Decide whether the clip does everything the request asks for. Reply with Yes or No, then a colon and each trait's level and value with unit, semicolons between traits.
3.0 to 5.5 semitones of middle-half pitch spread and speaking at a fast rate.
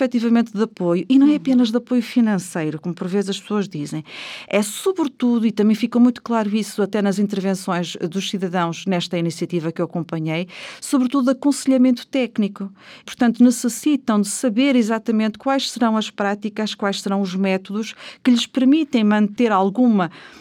No: average, 4.2 semitones; average, 165 wpm